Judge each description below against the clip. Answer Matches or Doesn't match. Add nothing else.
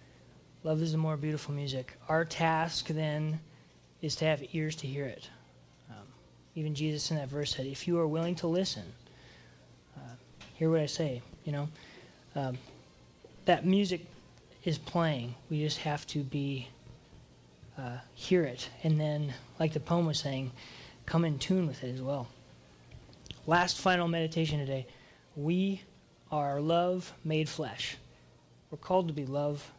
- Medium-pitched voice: Matches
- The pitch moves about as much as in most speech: Matches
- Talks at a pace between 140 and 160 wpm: Matches